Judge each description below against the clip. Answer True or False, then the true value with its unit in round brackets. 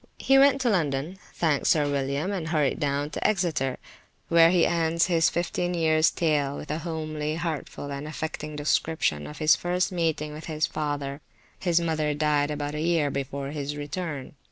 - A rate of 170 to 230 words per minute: True (175 wpm)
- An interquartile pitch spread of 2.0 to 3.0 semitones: True (2.5 semitones)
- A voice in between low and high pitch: True (155 Hz)